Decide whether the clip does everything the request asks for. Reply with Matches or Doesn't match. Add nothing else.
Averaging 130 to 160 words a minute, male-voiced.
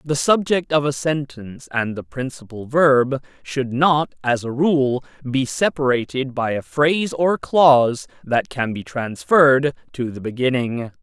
Matches